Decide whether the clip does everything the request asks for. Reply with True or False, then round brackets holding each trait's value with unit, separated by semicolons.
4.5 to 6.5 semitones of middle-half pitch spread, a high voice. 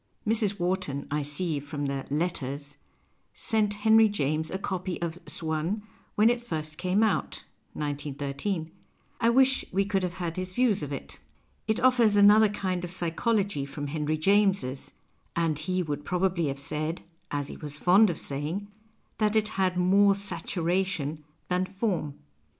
False (5.1 semitones; 180 Hz)